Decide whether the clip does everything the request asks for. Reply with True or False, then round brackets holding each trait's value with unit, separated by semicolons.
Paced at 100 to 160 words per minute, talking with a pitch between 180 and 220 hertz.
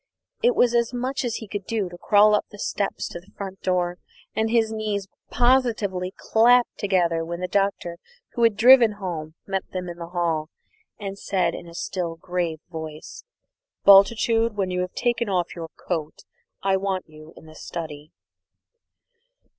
False (170 wpm; 190 Hz)